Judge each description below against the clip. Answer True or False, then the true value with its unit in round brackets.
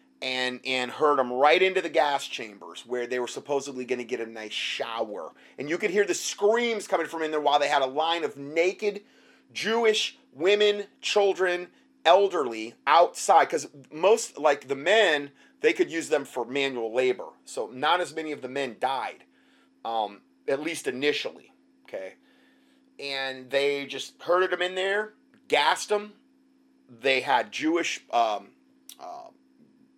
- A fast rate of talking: False (160 wpm)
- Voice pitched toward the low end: False (170 Hz)